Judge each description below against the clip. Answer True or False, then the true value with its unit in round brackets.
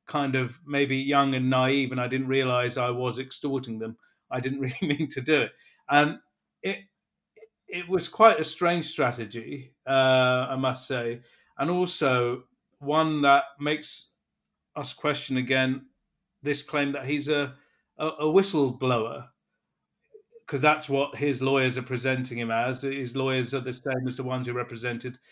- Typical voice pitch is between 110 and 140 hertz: True (135 Hz)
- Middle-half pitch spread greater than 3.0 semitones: False (2.7 semitones)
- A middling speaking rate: True (160 wpm)